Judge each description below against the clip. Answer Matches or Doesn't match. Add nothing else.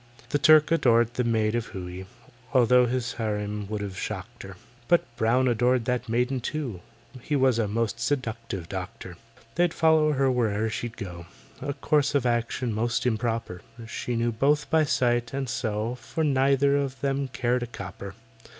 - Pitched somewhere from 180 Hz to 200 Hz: Doesn't match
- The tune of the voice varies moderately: Matches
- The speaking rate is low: Doesn't match